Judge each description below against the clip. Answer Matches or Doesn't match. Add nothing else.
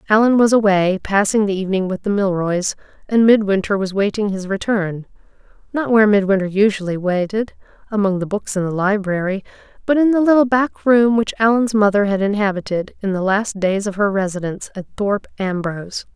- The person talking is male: Doesn't match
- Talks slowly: Doesn't match